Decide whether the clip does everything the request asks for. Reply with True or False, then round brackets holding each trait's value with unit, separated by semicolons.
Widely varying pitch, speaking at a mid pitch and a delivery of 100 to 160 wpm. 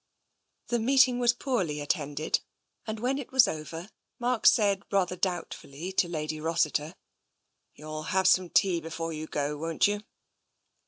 True (5.9 semitones; 175 Hz; 145 wpm)